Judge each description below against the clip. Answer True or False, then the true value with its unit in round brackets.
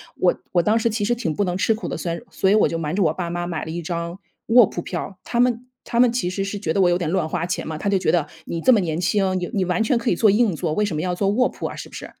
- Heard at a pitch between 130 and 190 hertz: True (185 Hz)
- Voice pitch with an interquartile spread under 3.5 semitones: False (3.8 semitones)